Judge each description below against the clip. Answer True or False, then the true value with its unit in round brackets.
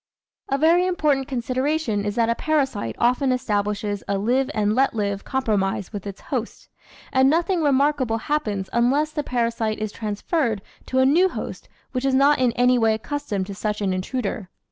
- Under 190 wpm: True (180 wpm)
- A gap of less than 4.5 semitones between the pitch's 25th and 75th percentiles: False (4.9 semitones)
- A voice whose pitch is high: True (245 Hz)